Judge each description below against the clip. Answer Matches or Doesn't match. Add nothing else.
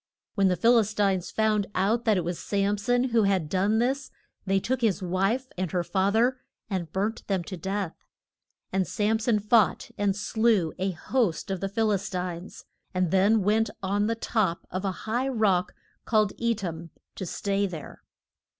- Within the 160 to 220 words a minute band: Matches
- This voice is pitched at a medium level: Doesn't match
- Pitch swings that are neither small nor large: Matches